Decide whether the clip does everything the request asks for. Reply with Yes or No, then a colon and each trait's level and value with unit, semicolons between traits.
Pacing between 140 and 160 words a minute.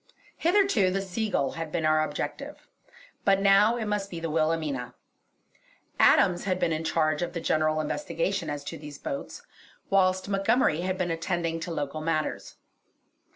Yes: average, 155 wpm